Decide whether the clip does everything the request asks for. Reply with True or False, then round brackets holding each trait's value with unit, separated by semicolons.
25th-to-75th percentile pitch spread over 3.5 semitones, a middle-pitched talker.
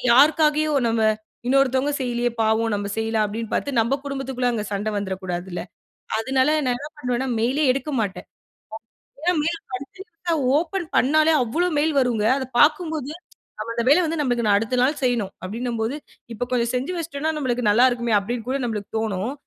False (4.7 semitones; 250 Hz)